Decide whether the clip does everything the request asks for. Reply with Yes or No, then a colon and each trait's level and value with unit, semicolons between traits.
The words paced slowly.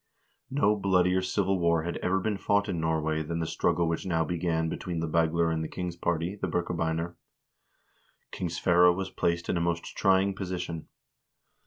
No: average, 175 wpm